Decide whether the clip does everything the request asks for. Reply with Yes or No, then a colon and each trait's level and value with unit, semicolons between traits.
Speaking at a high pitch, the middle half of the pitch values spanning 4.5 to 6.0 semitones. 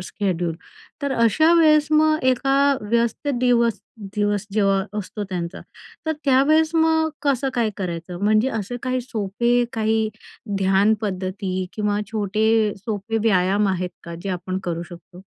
Yes: high, 215 Hz; average, 4.8 semitones